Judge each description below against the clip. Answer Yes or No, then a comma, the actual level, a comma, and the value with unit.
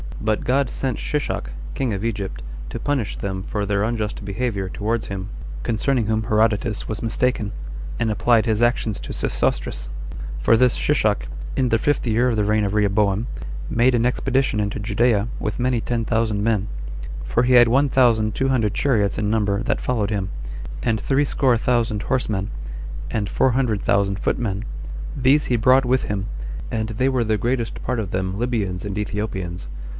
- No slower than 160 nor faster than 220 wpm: Yes, average, 175 wpm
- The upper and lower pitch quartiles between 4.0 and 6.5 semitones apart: No, average, 3.3 semitones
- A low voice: Yes, low, 110 Hz